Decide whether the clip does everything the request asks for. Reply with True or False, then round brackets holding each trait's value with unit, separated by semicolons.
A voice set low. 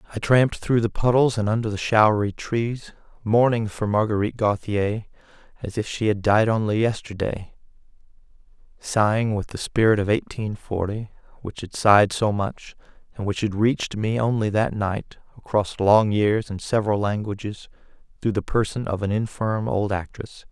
True (105 Hz)